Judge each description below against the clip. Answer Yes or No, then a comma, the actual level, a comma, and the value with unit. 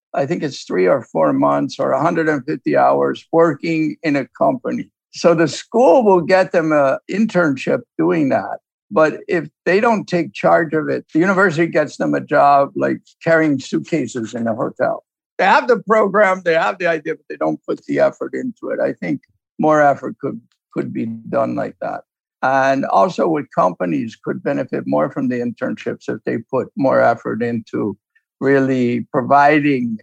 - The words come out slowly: No, average, 175 wpm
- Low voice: No, medium, 155 Hz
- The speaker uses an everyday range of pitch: Yes, average, 4.7 semitones